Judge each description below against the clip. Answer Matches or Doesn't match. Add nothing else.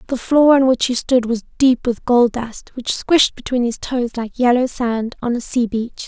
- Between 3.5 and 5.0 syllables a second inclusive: Matches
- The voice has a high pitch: Matches